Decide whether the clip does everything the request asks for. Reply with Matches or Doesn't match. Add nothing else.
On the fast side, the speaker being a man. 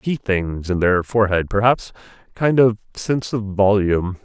Doesn't match